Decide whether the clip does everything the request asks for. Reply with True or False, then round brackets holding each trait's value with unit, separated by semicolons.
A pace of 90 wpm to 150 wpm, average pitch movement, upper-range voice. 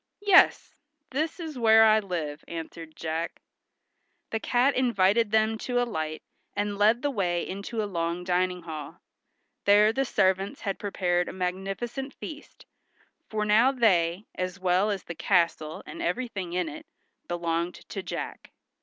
True (145 wpm; 4.5 semitones; 195 Hz)